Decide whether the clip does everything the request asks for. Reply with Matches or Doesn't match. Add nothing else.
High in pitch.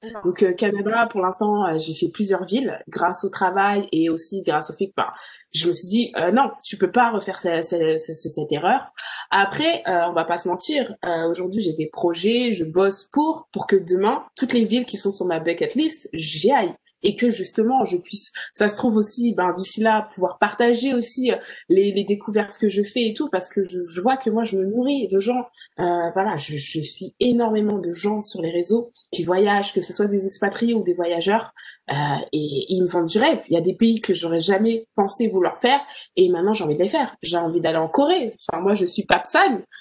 Matches